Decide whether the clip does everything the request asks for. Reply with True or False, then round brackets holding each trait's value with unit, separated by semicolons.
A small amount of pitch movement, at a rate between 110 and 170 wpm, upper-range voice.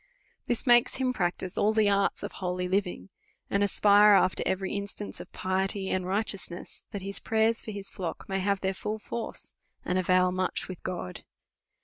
False (2.1 semitones; 180 wpm; 195 Hz)